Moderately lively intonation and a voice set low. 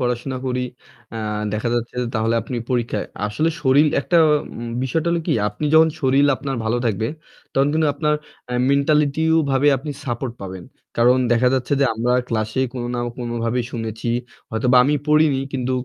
Yes: average, 3.4 semitones; low, 125 Hz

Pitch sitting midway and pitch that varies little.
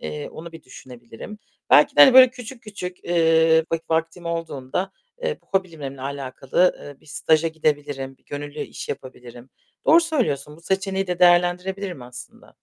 No: medium, 165 Hz; average, 5.1 semitones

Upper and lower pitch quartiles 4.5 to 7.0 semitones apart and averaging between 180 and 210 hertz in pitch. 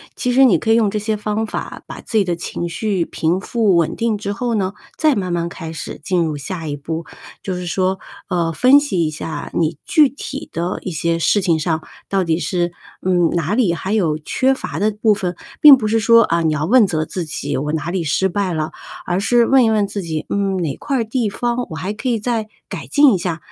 Yes: average, 4.8 semitones; high, 190 Hz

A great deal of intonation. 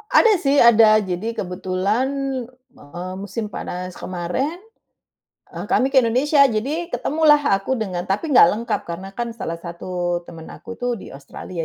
Yes: wide, 6.2 semitones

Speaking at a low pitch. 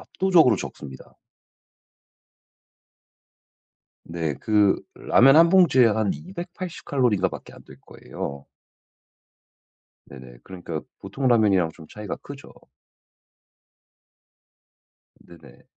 Yes: low, 105 Hz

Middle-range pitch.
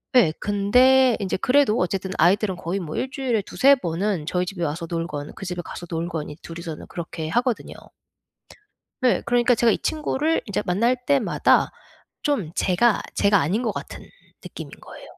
No: high, 200 Hz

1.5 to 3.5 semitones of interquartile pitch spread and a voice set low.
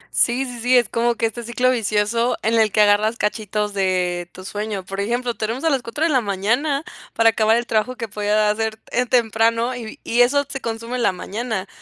No: average, 2.7 semitones; high, 225 Hz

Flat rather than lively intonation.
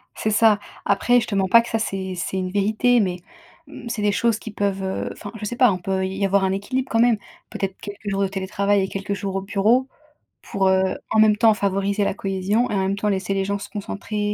Yes: narrow, 2.1 semitones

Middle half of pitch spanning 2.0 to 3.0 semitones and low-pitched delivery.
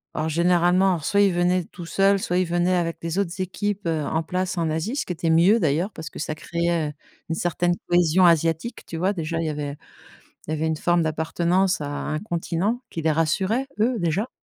No: narrow, 2.6 semitones; medium, 175 Hz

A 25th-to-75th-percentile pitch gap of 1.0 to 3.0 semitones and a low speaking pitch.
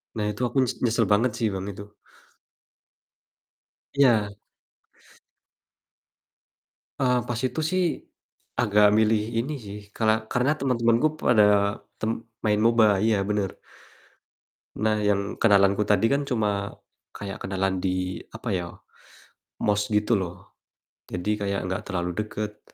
Yes: narrow, 2.5 semitones; low, 105 Hz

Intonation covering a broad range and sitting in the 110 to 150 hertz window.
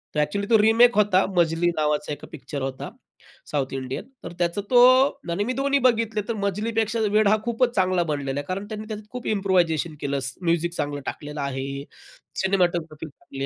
No: wide, 6.4 semitones; medium, 180 Hz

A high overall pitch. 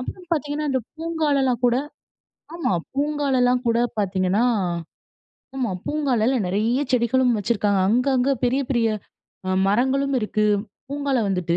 Yes: very high, 250 Hz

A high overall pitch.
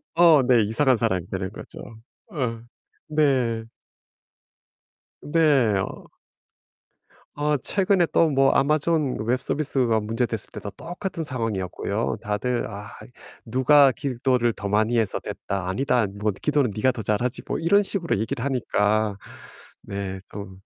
No: low, 120 Hz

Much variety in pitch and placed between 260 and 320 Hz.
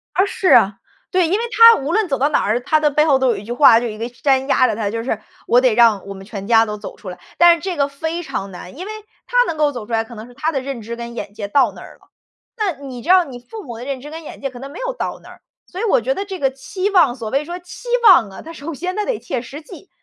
Yes: wide, 6.5 semitones; very high, 270 Hz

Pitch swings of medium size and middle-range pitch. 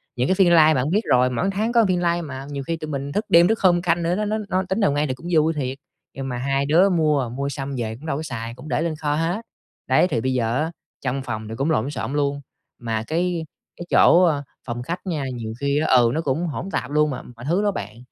Yes: average, 4.8 semitones; medium, 150 Hz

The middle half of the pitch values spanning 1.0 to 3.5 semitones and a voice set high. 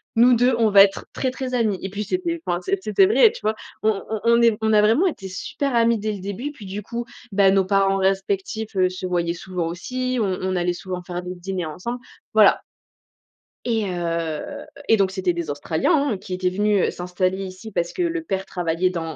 No: average, 3.9 semitones; high, 195 Hz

